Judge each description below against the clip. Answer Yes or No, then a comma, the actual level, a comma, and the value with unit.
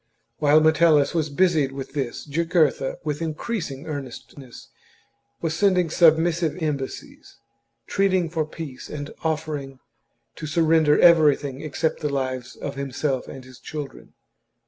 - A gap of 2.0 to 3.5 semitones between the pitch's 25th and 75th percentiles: Yes, average, 2.9 semitones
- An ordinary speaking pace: No, slow, 125 wpm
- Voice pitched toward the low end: No, medium, 150 Hz